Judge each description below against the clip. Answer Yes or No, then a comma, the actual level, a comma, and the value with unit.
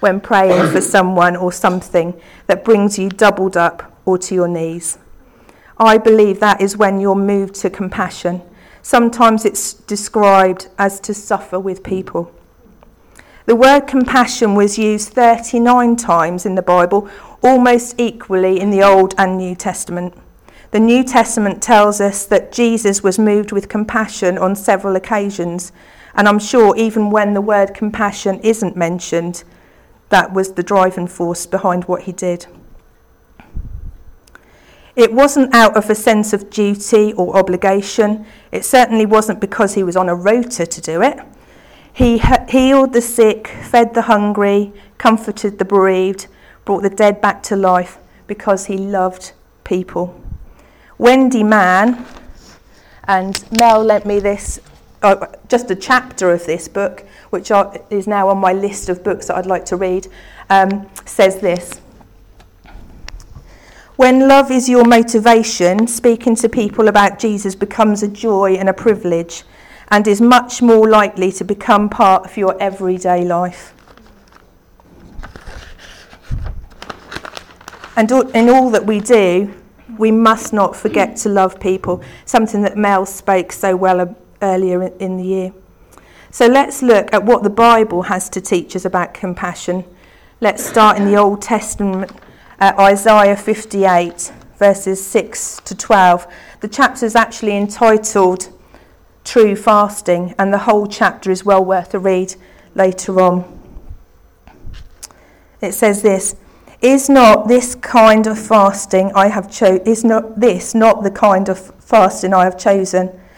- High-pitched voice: Yes, high, 200 Hz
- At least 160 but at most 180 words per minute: No, average, 145 wpm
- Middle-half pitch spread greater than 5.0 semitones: No, average, 2.9 semitones